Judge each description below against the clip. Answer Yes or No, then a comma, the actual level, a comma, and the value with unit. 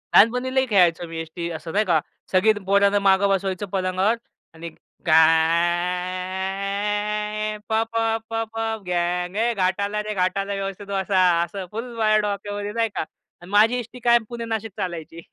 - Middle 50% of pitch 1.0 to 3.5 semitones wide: Yes, average, 2.9 semitones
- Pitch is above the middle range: Yes, high, 195 Hz